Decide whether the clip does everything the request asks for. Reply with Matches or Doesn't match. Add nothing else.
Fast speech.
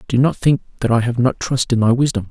Matches